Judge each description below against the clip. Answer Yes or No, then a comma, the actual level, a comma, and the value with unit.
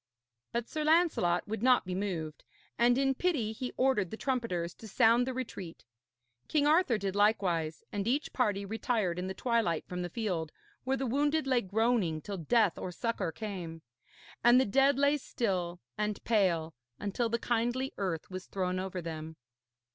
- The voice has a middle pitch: No, high, 215 Hz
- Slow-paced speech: No, average, 170 wpm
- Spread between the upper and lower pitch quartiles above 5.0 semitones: Yes, wide, 5.6 semitones